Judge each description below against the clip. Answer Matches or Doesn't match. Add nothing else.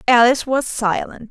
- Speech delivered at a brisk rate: Doesn't match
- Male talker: Doesn't match